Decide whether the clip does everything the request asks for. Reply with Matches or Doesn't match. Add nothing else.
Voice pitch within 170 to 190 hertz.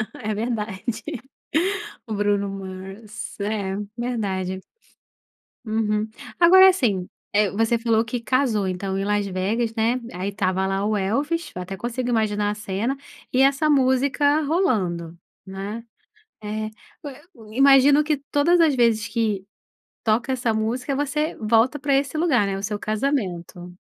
Doesn't match